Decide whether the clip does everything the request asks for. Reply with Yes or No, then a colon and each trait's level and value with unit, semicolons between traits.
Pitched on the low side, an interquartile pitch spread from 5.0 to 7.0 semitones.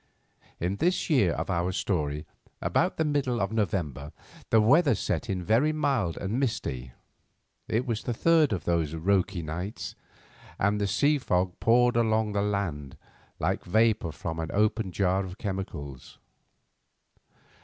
Yes: low, 100 Hz; average, 5.3 semitones